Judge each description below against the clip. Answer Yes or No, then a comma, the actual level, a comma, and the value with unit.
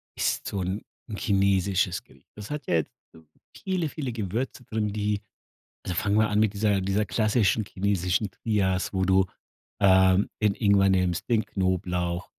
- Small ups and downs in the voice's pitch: Yes, narrow, 2.3 semitones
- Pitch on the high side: No, low, 100 Hz